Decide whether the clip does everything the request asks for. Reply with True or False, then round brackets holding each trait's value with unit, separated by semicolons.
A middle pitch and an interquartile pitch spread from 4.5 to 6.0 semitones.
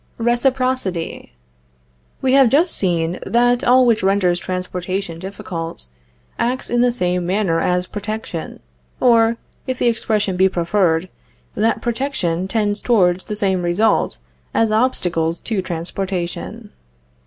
False (200 Hz; 4.9 semitones)